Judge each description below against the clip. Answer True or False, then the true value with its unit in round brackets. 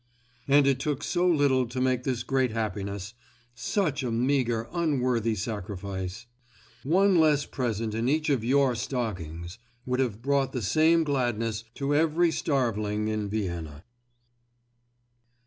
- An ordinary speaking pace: False (130 wpm)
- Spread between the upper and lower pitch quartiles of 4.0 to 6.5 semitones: True (4.6 semitones)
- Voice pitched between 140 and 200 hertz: False (125 Hz)